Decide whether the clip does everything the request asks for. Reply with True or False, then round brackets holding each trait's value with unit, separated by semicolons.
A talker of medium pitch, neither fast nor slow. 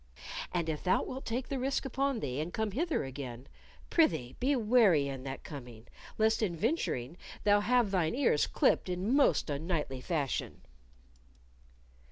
True (180 Hz; 155 wpm)